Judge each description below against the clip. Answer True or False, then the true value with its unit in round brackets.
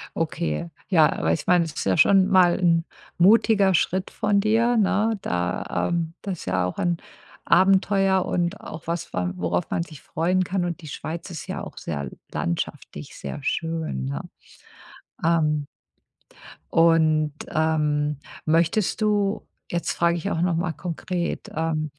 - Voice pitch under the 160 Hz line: False (170 Hz)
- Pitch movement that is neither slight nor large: True (3.5 semitones)